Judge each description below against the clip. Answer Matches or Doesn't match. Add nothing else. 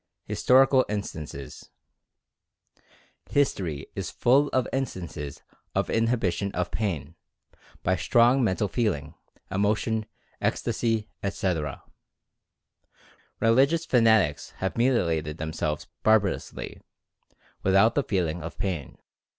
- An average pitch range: Doesn't match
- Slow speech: Matches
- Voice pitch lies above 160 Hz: Doesn't match